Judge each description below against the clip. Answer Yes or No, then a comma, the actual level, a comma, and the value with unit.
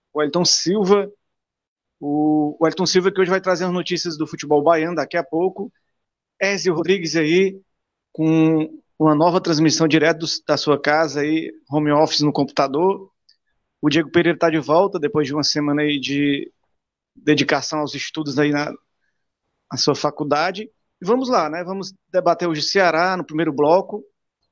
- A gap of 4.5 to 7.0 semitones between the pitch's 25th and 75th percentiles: No, average, 3.5 semitones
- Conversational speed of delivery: Yes, average, 165 wpm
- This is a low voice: No, medium, 160 Hz